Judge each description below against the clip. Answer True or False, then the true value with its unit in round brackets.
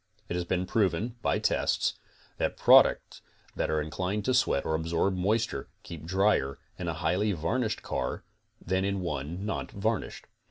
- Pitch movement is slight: False (4.2 semitones)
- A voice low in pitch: True (90 Hz)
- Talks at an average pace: True (160 wpm)